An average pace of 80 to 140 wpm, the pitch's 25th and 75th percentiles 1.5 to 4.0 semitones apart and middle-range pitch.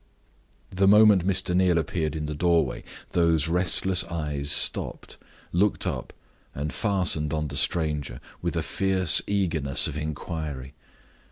No: slow, 135 wpm; average, 3.6 semitones; very low, 85 Hz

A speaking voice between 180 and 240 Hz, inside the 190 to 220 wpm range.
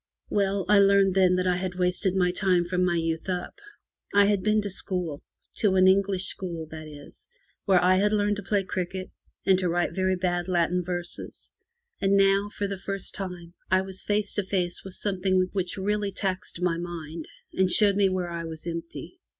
Yes: medium, 185 Hz; fast, 205 wpm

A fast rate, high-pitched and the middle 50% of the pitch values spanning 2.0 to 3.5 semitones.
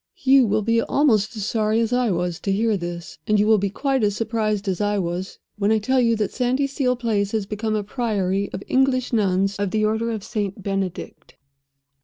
Yes: fast, 210 wpm; high, 215 Hz; average, 2.7 semitones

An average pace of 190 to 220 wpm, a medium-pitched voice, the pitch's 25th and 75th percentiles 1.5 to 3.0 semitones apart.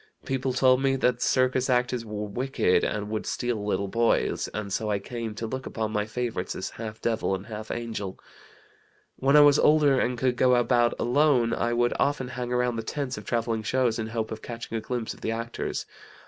No: fast, 205 wpm; low, 120 Hz; narrow, 2.6 semitones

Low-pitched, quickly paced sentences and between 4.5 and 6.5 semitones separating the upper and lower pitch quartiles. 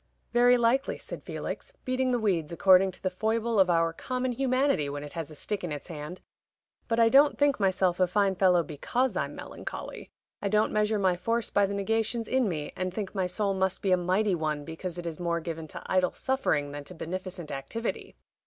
No: high, 190 Hz; fast, 210 wpm; average, 5.1 semitones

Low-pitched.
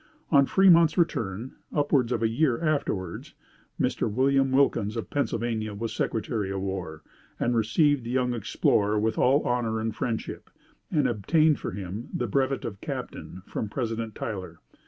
Yes: low, 115 Hz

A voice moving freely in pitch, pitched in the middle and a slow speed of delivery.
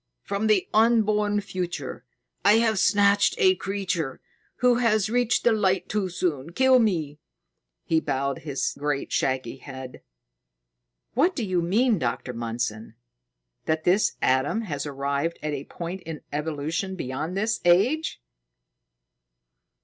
Yes: wide, 6.9 semitones; medium, 180 Hz; slow, 130 wpm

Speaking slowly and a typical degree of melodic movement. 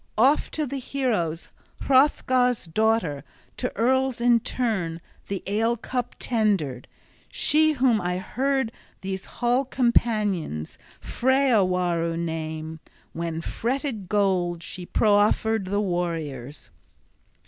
No: slow, 105 wpm; wide, 6.5 semitones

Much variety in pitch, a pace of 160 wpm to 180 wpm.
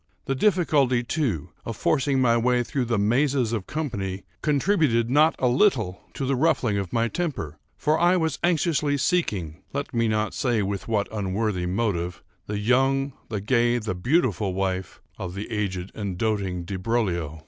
Yes: wide, 5.8 semitones; average, 170 wpm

